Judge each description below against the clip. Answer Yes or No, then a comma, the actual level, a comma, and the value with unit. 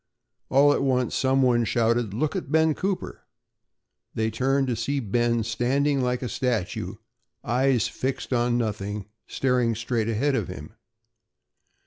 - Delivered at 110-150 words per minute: Yes, average, 140 wpm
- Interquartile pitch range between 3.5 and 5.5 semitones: No, average, 2.9 semitones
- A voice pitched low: Yes, low, 125 Hz